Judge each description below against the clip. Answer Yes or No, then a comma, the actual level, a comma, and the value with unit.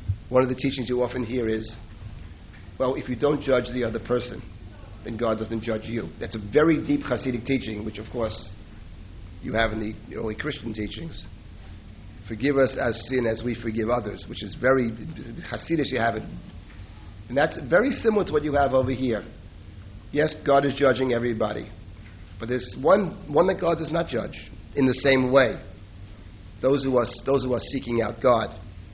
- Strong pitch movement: No, average, 4.3 semitones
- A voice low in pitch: Yes, low, 115 Hz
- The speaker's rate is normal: Yes, average, 185 wpm